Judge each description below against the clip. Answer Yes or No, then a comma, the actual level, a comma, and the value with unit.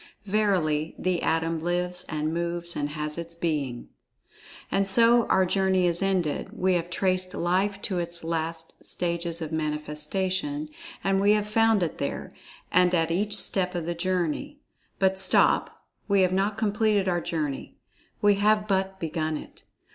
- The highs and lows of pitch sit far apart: No, average, 3.0 semitones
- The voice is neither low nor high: Yes, medium, 180 Hz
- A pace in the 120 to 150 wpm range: Yes, average, 145 wpm